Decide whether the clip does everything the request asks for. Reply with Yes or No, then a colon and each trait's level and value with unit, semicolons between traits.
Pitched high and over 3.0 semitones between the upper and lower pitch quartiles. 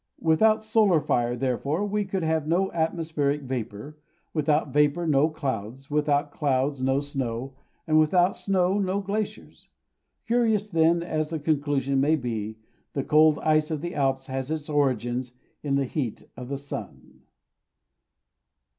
No: medium, 150 Hz; average, 3.7 semitones